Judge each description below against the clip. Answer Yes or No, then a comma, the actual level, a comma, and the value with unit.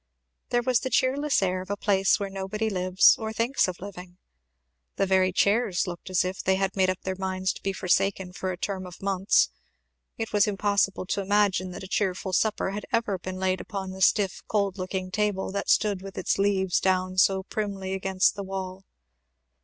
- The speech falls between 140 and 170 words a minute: No, average, 200 wpm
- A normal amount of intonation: No, narrow, 1.5 semitones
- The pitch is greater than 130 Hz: Yes, high, 190 Hz